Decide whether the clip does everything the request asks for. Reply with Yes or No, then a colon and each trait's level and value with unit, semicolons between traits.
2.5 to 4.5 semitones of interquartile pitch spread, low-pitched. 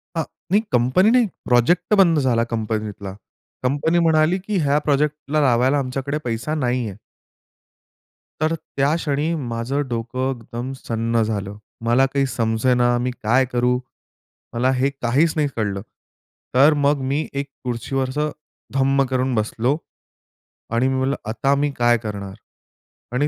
Yes: average, 3.7 semitones; low, 130 Hz